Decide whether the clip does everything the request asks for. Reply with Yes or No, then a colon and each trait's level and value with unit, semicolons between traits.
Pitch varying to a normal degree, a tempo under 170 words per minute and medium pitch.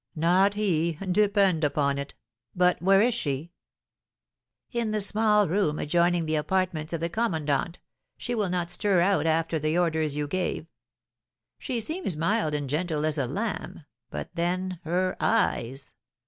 Yes: average, 4.1 semitones; average, 150 wpm; medium, 175 Hz